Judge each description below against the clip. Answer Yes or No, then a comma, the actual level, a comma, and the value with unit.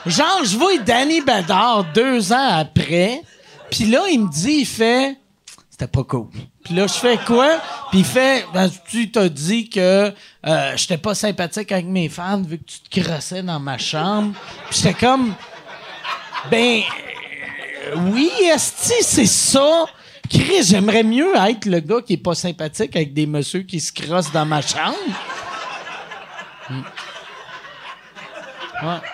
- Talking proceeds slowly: No, average, 155 wpm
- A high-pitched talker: Yes, high, 200 Hz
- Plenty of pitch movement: Yes, wide, 5.9 semitones